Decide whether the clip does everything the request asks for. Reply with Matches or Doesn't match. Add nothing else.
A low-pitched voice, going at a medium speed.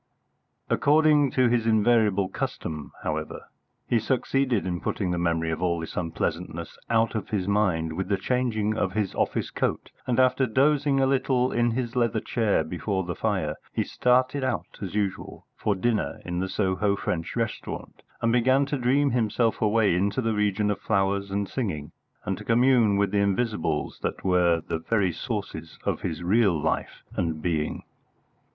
Matches